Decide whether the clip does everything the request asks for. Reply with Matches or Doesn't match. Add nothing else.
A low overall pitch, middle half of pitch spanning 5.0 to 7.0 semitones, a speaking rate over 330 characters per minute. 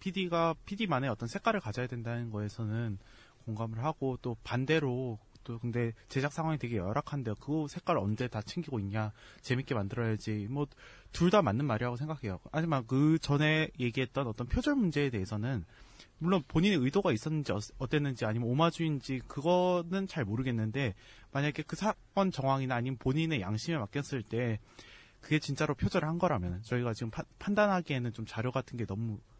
Matches